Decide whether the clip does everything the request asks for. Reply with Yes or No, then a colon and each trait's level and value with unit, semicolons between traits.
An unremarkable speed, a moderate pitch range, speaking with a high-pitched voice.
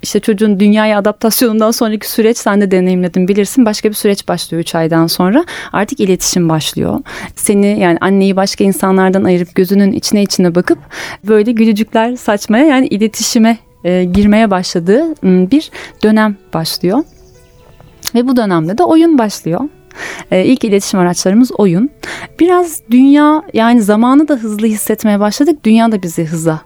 No: fast, 145 wpm; average, 3.7 semitones; high, 210 Hz